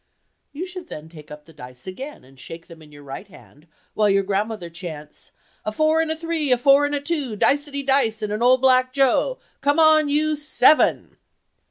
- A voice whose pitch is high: Yes, very high, 255 Hz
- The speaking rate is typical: Yes, average, 190 wpm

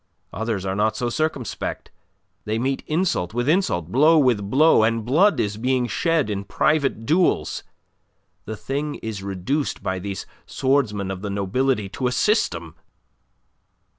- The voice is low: Yes, low, 115 Hz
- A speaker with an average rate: Yes, average, 145 wpm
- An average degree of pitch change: No, wide, 6.0 semitones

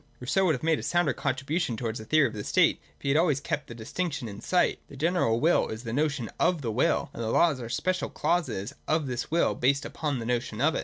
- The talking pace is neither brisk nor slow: No, fast, 265 wpm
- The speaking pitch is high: No, medium, 140 Hz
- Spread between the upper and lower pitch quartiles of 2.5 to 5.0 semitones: No, wide, 5.4 semitones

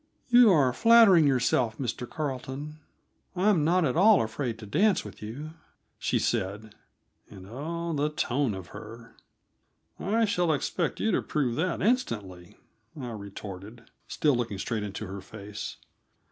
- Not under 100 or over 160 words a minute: Yes, average, 145 wpm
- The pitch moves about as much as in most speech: No, wide, 7.6 semitones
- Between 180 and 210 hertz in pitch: No, low, 130 Hz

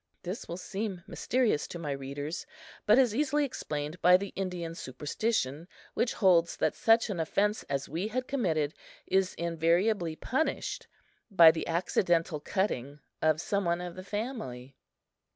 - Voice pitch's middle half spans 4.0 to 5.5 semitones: Yes, average, 4.9 semitones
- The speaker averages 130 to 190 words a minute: Yes, average, 150 wpm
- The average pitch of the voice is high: No, medium, 175 Hz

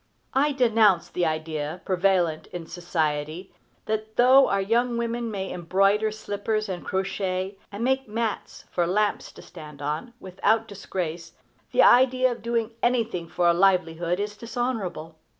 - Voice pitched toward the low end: No, high, 195 Hz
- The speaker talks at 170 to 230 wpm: No, average, 145 wpm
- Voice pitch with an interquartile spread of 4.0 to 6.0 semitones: Yes, average, 4.7 semitones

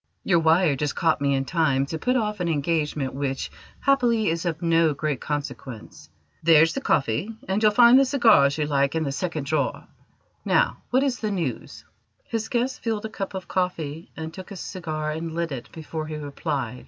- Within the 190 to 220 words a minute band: Yes, average, 195 wpm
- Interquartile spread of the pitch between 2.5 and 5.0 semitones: No, wide, 5.4 semitones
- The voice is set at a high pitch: No, medium, 160 Hz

